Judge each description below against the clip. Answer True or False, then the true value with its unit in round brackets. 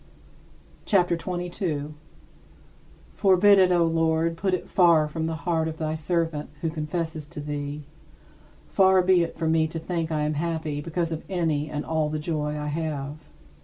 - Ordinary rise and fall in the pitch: False (2.2 semitones)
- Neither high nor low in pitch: True (160 Hz)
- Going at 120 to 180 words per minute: True (170 wpm)